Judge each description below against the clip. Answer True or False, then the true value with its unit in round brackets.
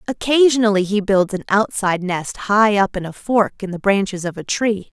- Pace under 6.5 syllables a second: True (5.1 syllables/s)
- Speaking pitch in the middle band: False (200 Hz)